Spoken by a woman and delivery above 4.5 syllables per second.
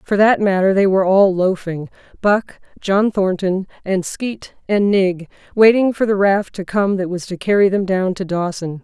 Yes: female; 4.7 syllables/s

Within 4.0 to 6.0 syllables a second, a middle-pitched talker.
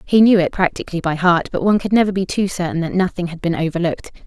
No: 7.0 syllables/s; medium, 180 Hz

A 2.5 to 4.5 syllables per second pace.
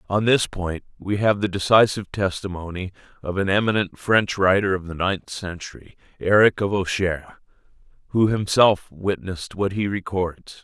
No: 4.9 syllables/s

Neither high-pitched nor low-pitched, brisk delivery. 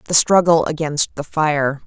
No: medium, 155 Hz; average, 160 wpm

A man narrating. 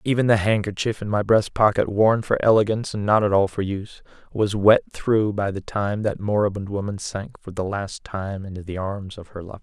Yes: male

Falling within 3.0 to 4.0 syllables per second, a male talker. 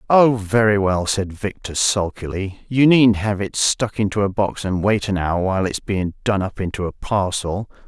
No: 4.6 syllables/s; male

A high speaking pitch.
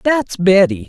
Yes: high, 200 Hz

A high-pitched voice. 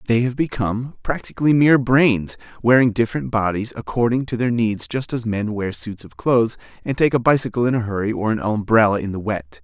No: low, 115 Hz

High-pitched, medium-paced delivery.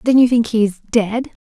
Yes: high, 225 Hz; average, 170 wpm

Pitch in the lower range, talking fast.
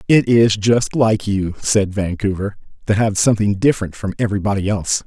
No: low, 105 Hz; average, 165 wpm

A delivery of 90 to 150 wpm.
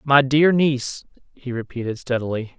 Yes: average, 140 wpm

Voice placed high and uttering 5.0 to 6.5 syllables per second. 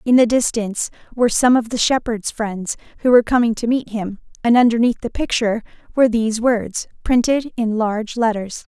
Yes: high, 230 Hz; 5.7 syllables/s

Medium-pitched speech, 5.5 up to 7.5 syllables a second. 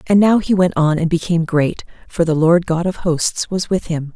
No: medium, 170 Hz; 5.0 syllables/s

